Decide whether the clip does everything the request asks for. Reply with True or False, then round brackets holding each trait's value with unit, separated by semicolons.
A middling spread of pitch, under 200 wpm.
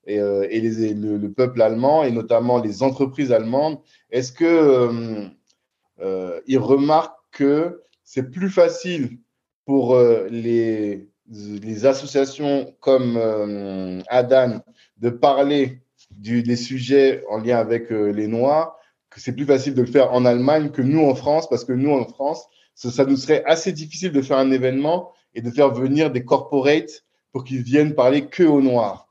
True (3.7 semitones; 170 wpm)